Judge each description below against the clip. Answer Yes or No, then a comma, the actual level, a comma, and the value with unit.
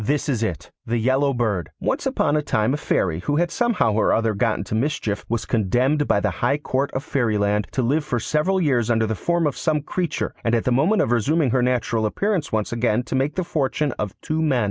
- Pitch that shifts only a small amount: No, average, 5.1 semitones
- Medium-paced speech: No, fast, 235 wpm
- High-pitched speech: No, low, 125 Hz